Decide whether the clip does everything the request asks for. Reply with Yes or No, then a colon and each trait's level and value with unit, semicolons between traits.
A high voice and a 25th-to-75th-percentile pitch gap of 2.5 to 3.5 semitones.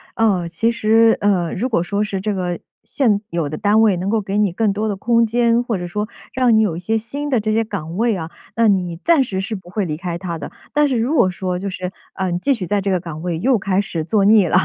No: high, 200 Hz; average, 3.9 semitones